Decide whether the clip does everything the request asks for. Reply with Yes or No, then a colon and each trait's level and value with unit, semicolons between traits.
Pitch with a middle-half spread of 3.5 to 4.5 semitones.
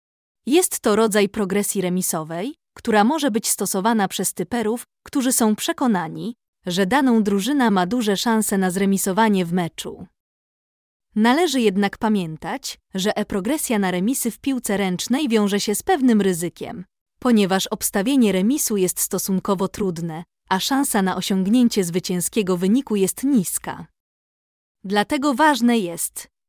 Yes: average, 4.1 semitones